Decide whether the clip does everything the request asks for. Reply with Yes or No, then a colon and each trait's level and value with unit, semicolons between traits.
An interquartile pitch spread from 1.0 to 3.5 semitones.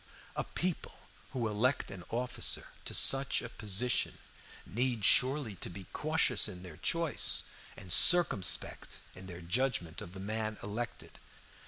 No: wide, 5.6 semitones